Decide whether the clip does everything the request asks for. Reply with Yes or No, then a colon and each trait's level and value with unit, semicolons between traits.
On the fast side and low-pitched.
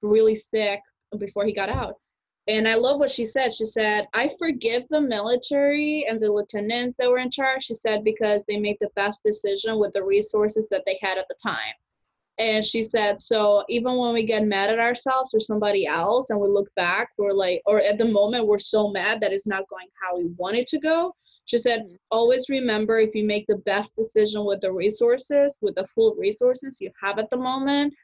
No: fast, 215 wpm; high, 220 Hz